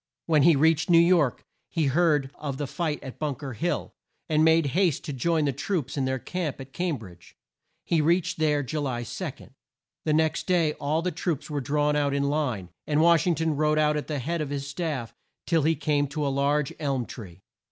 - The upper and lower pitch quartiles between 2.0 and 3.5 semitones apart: Yes, average, 2.7 semitones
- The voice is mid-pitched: Yes, medium, 150 Hz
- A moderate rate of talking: No, fast, 215 wpm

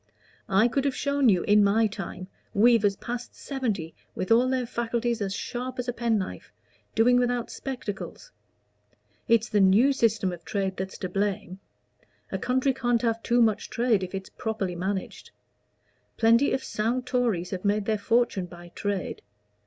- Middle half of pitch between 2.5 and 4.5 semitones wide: Yes, average, 3.9 semitones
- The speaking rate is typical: Yes, average, 165 wpm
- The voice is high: Yes, high, 225 Hz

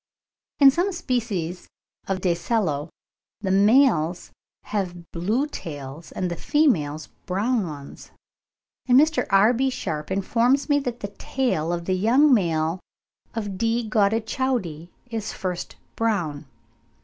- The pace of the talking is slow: Yes, slow, 125 wpm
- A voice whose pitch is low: No, high, 200 Hz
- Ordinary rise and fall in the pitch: No, wide, 6.3 semitones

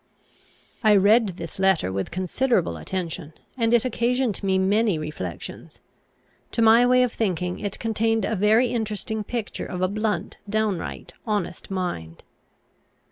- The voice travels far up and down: No, average, 3.7 semitones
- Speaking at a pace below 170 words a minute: Yes, slow, 135 wpm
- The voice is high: Yes, high, 210 Hz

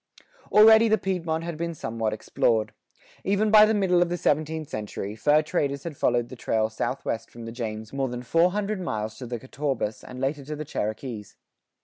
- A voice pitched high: No, medium, 140 Hz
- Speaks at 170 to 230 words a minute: Yes, average, 195 wpm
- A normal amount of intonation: No, wide, 7.0 semitones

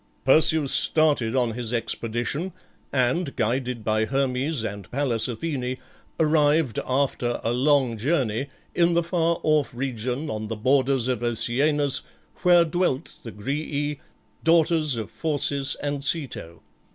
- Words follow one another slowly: Yes, slow, 130 wpm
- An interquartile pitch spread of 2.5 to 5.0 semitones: Yes, average, 4.3 semitones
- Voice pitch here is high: No, low, 135 Hz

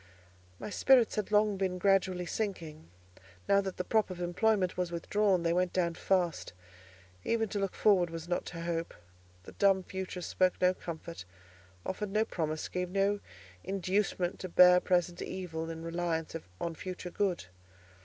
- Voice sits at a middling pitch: Yes, medium, 180 Hz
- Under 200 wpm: Yes, average, 160 wpm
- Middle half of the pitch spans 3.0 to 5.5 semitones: No, narrow, 2.4 semitones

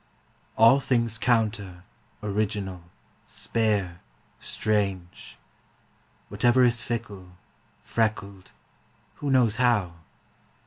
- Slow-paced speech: Yes, slow, 75 wpm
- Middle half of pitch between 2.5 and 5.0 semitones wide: Yes, average, 3.4 semitones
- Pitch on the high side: No, low, 110 Hz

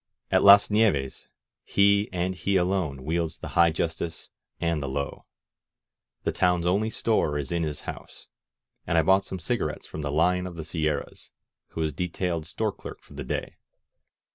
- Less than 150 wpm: No, average, 175 wpm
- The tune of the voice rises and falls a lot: No, average, 3.2 semitones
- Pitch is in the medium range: No, very low, 85 Hz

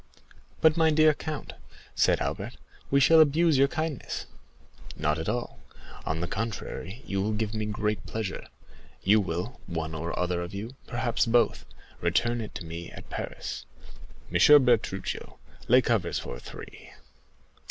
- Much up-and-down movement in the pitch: Yes, wide, 6.8 semitones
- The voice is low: Yes, low, 110 Hz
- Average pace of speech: Yes, average, 150 wpm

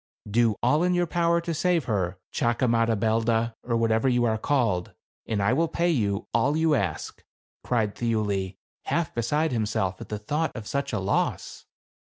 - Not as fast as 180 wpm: Yes, average, 170 wpm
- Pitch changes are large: Yes, wide, 5.8 semitones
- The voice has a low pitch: Yes, low, 115 Hz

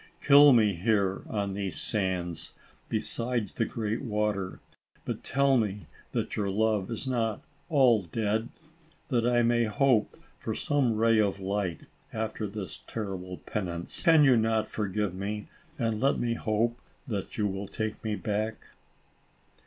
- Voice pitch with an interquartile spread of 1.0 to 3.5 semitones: Yes, average, 2.8 semitones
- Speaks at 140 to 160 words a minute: Yes, average, 145 wpm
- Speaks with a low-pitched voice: Yes, low, 110 Hz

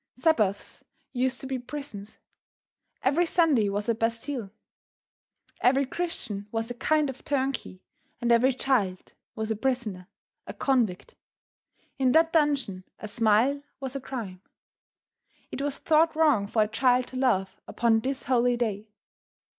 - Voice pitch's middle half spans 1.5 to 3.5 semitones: No, average, 4.2 semitones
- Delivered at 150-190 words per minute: No, average, 140 wpm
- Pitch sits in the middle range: No, high, 245 Hz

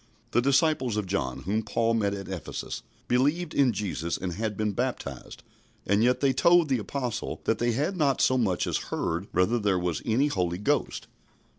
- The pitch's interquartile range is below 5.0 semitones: No, wide, 5.5 semitones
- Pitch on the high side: No, low, 115 Hz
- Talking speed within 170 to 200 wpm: Yes, average, 185 wpm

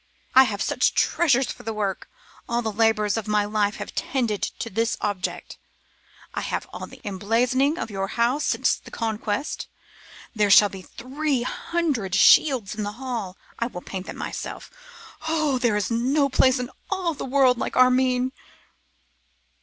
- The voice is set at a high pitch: Yes, high, 235 Hz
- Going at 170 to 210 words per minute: No, average, 160 wpm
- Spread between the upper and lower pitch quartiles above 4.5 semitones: No, average, 4.0 semitones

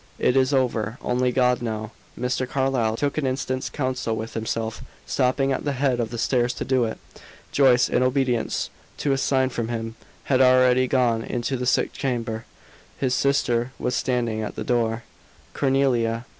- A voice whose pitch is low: Yes, low, 125 Hz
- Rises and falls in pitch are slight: Yes, narrow, 2.2 semitones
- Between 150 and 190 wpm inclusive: Yes, average, 170 wpm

